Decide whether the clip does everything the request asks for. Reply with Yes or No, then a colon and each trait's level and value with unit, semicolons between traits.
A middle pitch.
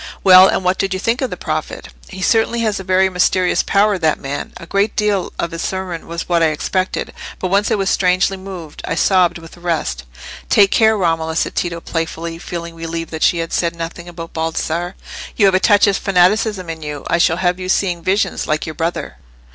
Yes: medium, 180 Hz